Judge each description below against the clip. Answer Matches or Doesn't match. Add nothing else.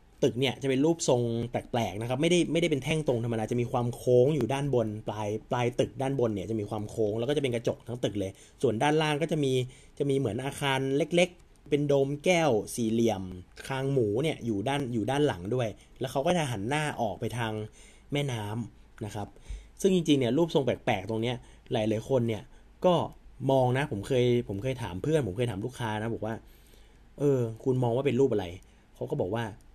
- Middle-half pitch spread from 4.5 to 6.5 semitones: Doesn't match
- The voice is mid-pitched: Doesn't match